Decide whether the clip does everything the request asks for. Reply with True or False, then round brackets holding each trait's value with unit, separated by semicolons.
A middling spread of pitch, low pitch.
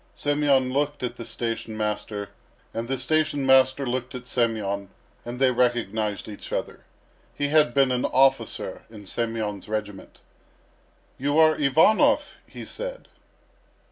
True (4.1 semitones; 125 Hz)